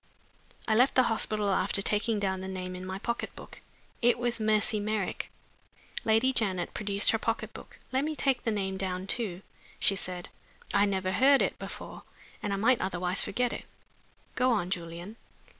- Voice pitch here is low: No, high, 205 Hz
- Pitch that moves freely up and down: No, average, 3.6 semitones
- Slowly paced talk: No, average, 175 wpm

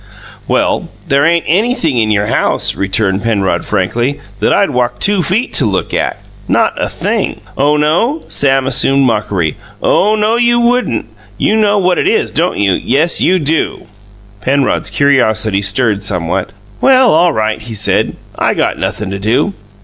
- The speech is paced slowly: No, average, 165 wpm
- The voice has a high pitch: No, low, 135 Hz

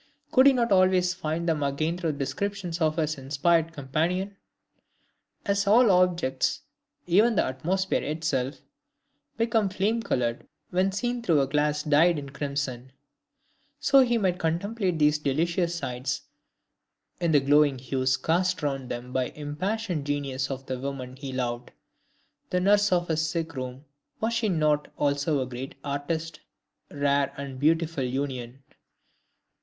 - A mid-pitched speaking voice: Yes, medium, 155 Hz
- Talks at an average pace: Yes, average, 145 wpm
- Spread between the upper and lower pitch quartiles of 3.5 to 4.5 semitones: No, average, 4.9 semitones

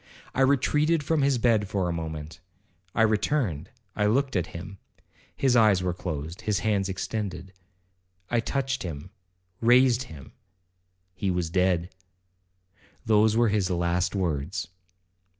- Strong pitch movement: No, average, 4.0 semitones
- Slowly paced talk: Yes, slow, 115 wpm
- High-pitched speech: No, very low, 95 Hz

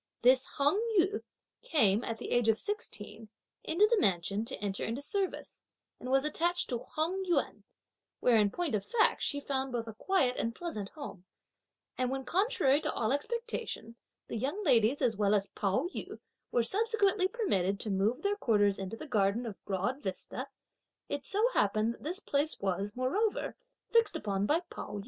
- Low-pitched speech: No, very high, 255 Hz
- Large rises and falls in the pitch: Yes, wide, 8.8 semitones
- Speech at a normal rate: Yes, average, 180 wpm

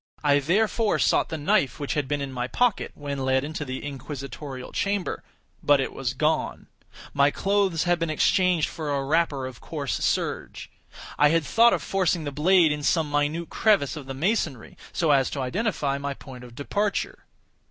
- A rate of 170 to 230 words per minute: Yes, average, 185 wpm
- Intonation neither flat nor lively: Yes, average, 3.7 semitones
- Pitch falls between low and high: Yes, medium, 145 Hz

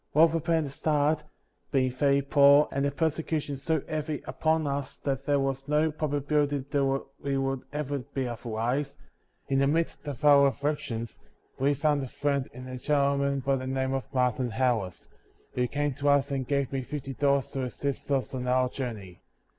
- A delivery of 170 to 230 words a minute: Yes, average, 185 wpm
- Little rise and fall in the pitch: Yes, narrow, 1.9 semitones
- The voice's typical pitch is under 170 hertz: Yes, medium, 140 Hz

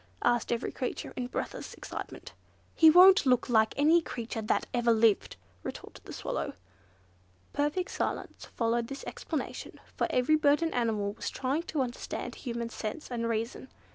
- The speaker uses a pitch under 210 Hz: No, high, 245 Hz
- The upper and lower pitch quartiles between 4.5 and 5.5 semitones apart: No, average, 4.1 semitones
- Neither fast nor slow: Yes, average, 155 wpm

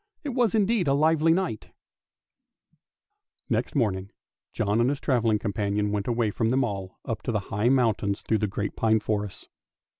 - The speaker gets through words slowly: No, average, 170 wpm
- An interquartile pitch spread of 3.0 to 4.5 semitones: No, average, 5.1 semitones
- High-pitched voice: No, low, 115 Hz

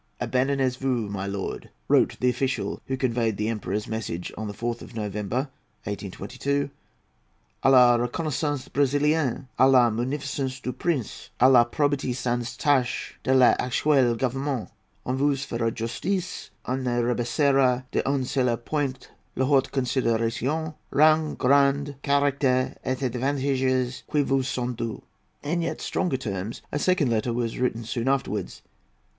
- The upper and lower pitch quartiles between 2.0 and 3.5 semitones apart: Yes, average, 2.9 semitones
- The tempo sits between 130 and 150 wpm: Yes, average, 140 wpm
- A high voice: No, low, 130 Hz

